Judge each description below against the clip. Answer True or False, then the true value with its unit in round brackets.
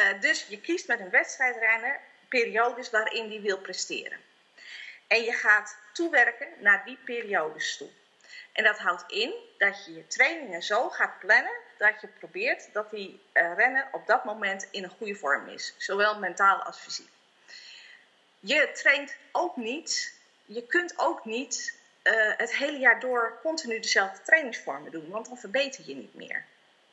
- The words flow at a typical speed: True (155 wpm)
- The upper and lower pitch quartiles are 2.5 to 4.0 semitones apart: False (5.4 semitones)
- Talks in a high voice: True (235 Hz)